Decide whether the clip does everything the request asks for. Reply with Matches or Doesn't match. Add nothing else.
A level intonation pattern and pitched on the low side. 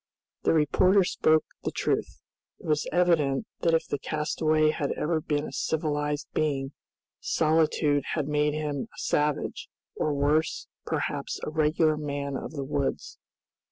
Doesn't match